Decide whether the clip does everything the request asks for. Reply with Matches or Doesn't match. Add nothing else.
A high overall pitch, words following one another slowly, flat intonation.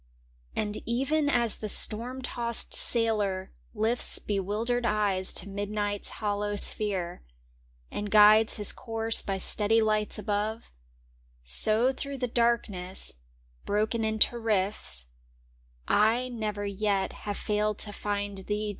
Matches